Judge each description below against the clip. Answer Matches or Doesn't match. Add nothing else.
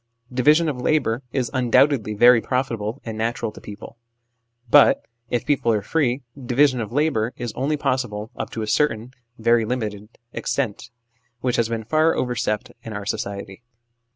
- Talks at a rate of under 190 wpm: Matches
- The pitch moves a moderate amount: Matches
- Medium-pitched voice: Doesn't match